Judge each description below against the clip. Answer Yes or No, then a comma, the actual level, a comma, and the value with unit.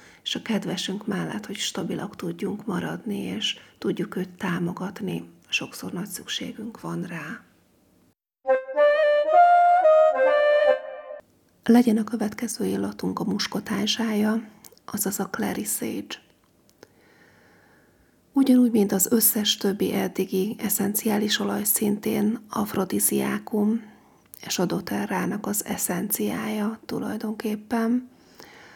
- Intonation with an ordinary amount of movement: Yes, average, 3.3 semitones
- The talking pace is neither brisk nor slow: No, slow, 90 wpm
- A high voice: Yes, high, 215 Hz